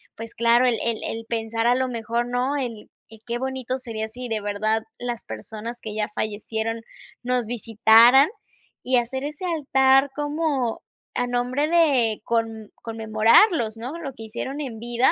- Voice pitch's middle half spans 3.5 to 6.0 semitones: No, average, 2.9 semitones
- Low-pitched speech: No, high, 235 Hz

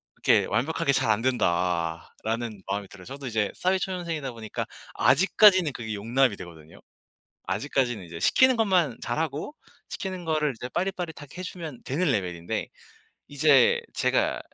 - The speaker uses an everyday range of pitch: No, wide, 8.2 semitones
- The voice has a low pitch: Yes, low, 130 Hz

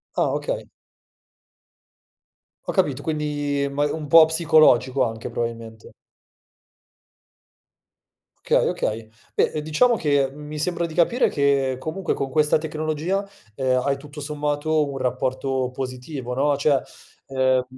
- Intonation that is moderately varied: Yes, average, 3.0 semitones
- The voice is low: No, medium, 145 Hz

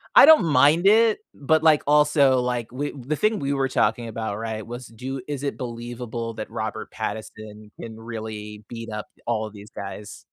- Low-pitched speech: Yes, low, 120 Hz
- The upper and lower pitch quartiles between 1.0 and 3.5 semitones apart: No, average, 4.5 semitones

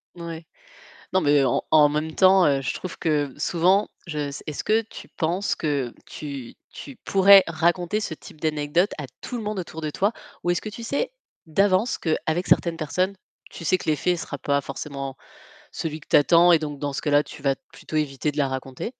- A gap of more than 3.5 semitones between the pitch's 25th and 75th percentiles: Yes, average, 4.1 semitones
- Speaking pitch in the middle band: Yes, medium, 160 Hz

